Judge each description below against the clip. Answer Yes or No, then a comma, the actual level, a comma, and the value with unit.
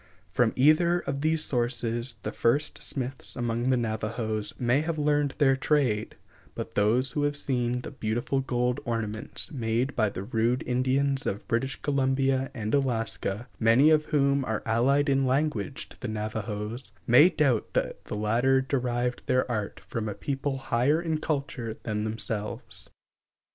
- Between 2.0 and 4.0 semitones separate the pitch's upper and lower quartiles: Yes, average, 3.6 semitones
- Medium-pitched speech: No, low, 125 Hz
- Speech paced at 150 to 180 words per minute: Yes, average, 155 wpm